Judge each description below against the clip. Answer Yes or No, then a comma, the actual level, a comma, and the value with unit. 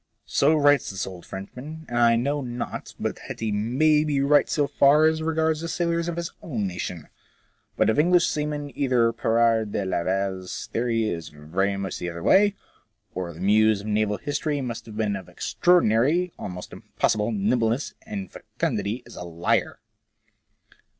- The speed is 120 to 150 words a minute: No, average, 165 wpm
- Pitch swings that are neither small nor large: No, wide, 7.0 semitones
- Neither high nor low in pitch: No, low, 115 Hz